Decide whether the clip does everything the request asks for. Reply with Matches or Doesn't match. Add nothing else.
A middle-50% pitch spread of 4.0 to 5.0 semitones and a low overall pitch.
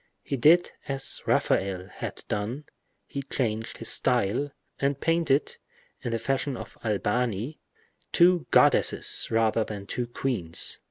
Matches